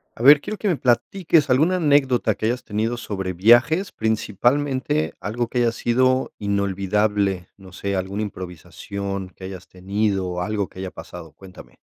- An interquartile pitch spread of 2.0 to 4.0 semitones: No, average, 5.0 semitones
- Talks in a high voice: No, low, 105 Hz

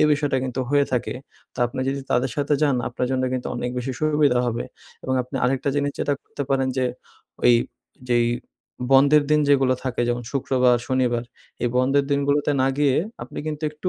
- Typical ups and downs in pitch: No, narrow, 2.2 semitones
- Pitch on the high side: No, low, 135 Hz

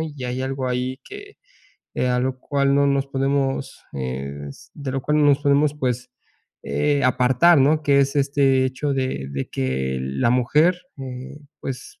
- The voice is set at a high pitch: No, low, 135 Hz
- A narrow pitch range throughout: Yes, narrow, 2.2 semitones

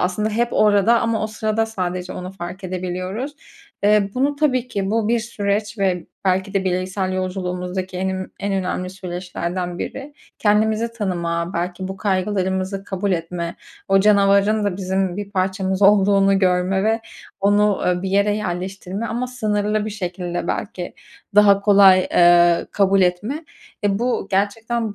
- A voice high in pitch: Yes, high, 195 Hz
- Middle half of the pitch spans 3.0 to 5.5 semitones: No, narrow, 2.4 semitones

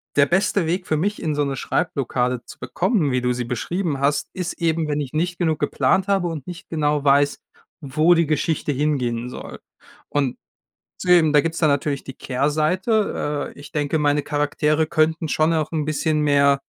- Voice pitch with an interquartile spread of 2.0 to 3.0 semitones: Yes, average, 2.7 semitones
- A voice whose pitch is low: No, medium, 150 Hz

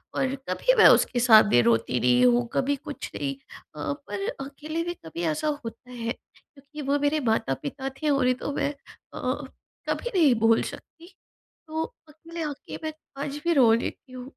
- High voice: Yes, very high, 270 Hz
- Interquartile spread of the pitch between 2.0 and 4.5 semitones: No, wide, 5.4 semitones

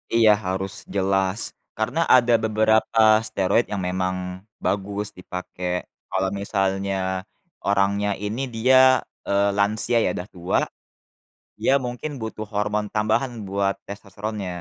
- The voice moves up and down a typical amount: No, narrow, 2.1 semitones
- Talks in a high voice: No, low, 100 Hz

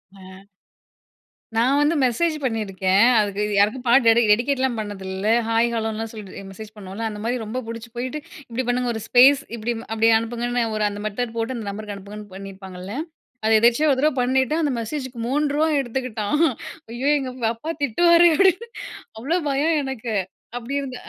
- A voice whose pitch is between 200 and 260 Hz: Yes, high, 235 Hz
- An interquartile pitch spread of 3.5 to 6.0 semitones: Yes, average, 3.8 semitones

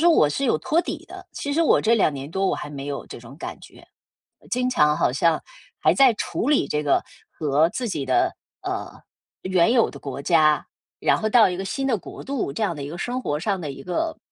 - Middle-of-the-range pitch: Yes, medium, 175 Hz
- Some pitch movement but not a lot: No, wide, 8.7 semitones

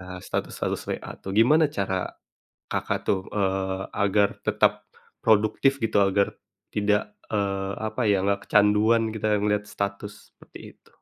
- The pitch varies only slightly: Yes, narrow, 1.7 semitones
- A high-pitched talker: No, low, 105 Hz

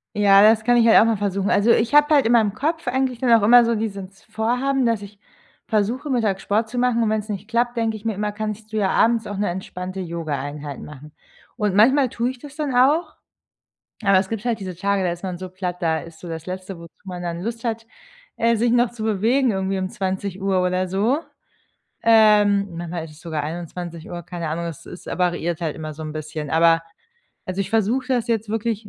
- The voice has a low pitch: No, high, 205 Hz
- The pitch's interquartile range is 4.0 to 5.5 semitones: Yes, average, 4.4 semitones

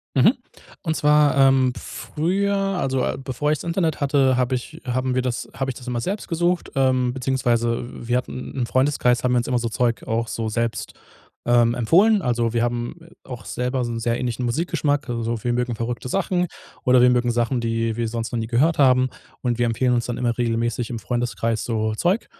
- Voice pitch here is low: Yes, low, 125 Hz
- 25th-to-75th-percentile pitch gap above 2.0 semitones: Yes, narrow, 2.5 semitones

